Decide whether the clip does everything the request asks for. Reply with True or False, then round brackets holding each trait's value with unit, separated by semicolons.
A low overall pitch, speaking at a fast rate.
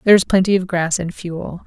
False (180 Hz; 255 wpm)